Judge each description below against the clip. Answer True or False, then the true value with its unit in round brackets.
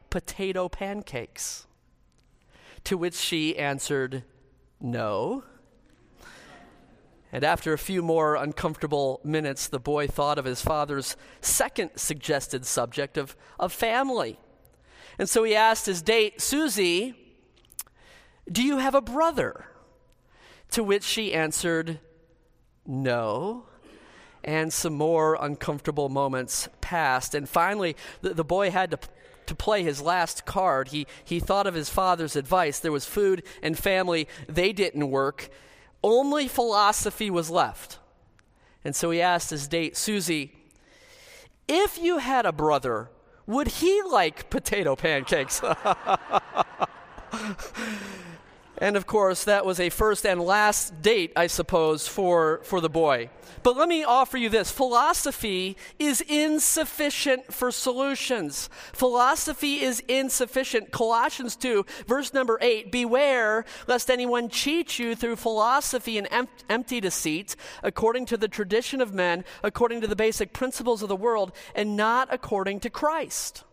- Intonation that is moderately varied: False (7.5 semitones)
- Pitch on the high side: True (200 Hz)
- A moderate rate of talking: False (130 wpm)